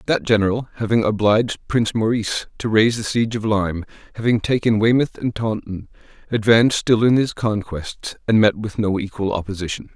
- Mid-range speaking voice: No, low, 110 Hz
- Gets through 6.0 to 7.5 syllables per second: No, 5.7 syllables/s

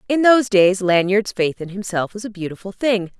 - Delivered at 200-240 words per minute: Yes, fast, 205 wpm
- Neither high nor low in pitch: No, high, 200 Hz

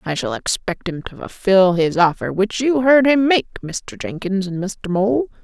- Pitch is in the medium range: No, high, 200 Hz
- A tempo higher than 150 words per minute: Yes, average, 200 wpm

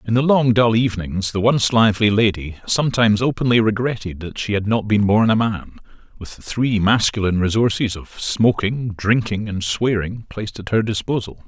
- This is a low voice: Yes, low, 105 Hz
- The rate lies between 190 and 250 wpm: No, average, 175 wpm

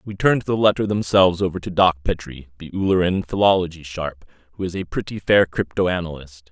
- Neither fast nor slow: Yes, average, 175 wpm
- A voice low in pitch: Yes, very low, 90 Hz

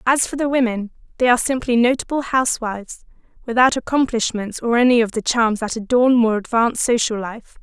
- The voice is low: No, high, 235 Hz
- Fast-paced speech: No, average, 175 wpm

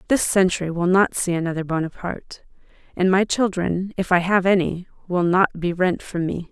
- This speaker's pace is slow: No, average, 185 wpm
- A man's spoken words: No, female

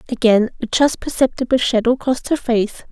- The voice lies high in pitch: Yes, high, 245 Hz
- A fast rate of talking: No, average, 165 wpm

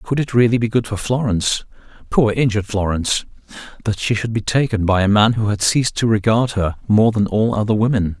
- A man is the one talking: Yes, male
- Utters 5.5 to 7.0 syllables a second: Yes, 5.8 syllables/s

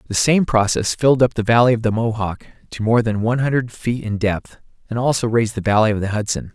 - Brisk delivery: Yes, fast, 240 wpm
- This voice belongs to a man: Yes, male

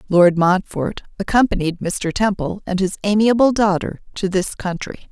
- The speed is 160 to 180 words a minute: No, average, 140 wpm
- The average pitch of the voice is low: No, high, 190 Hz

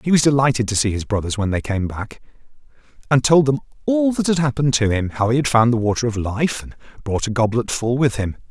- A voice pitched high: No, low, 125 Hz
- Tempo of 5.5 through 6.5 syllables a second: Yes, 6.1 syllables/s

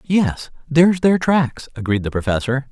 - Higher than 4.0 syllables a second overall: Yes, 4.6 syllables/s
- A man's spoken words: Yes, male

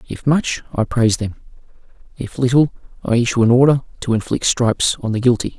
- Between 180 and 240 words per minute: Yes, average, 185 wpm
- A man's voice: Yes, male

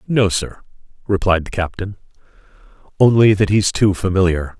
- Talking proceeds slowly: Yes, slow, 130 wpm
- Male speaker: Yes, male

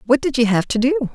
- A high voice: Yes, very high, 255 Hz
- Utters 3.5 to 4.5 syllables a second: No, 7.1 syllables/s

